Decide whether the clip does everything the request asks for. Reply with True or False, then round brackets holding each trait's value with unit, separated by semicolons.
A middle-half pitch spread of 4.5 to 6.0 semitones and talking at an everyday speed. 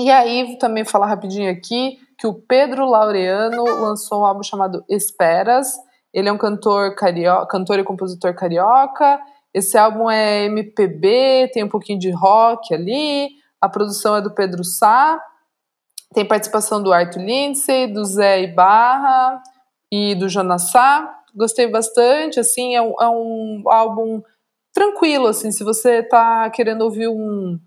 False (3.8 semitones; 145 wpm)